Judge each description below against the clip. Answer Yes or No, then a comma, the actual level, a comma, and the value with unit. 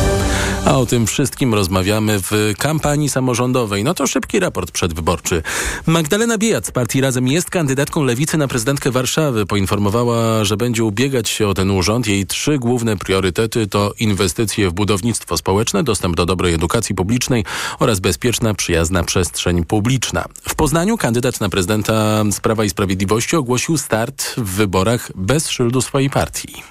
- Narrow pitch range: No, average, 4.3 semitones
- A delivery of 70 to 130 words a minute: No, average, 150 wpm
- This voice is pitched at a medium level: No, low, 115 Hz